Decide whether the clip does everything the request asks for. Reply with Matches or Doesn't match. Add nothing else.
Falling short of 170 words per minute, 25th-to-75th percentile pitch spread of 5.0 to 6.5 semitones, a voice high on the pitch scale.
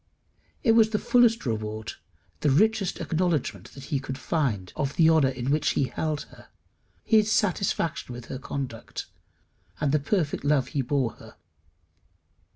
Doesn't match